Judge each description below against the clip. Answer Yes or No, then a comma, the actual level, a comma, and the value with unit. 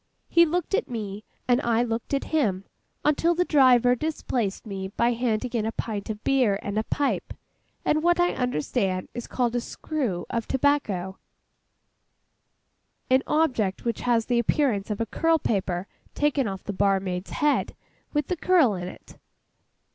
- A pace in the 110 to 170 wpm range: Yes, average, 155 wpm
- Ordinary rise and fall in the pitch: No, wide, 6.3 semitones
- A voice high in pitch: Yes, high, 235 Hz